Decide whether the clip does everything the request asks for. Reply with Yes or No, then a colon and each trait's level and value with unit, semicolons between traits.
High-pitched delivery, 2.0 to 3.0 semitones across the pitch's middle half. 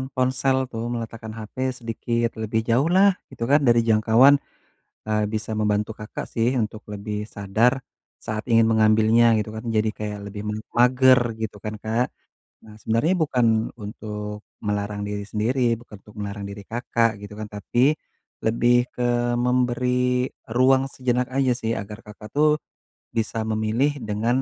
No: low, 110 Hz; narrow, 2.6 semitones